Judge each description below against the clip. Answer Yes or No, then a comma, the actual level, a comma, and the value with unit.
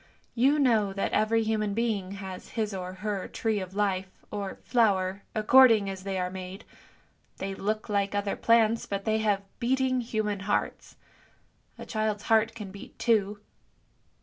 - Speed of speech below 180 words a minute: Yes, average, 155 wpm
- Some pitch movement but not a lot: No, narrow, 2.3 semitones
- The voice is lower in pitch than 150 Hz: No, high, 210 Hz